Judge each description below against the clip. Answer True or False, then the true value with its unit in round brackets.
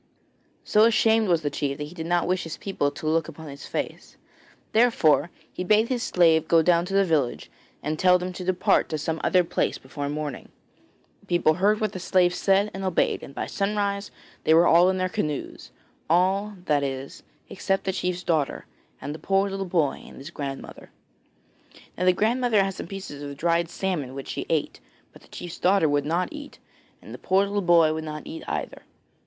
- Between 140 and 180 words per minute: False (205 wpm)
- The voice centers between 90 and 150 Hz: False (175 Hz)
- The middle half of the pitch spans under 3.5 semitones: False (3.9 semitones)